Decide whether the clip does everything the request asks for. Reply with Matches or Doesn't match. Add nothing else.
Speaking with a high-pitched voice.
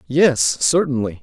Doesn't match